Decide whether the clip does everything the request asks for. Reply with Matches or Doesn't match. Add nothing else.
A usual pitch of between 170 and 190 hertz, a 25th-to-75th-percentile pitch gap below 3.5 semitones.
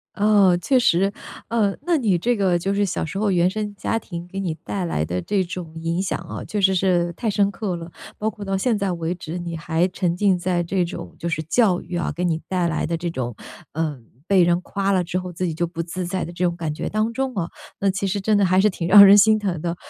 Matches